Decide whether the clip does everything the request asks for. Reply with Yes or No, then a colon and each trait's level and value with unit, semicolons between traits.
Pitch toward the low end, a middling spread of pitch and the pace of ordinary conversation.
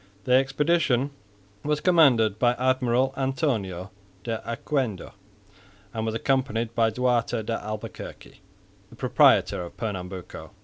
No: low, 120 Hz; average, 3.4 semitones; slow, 115 wpm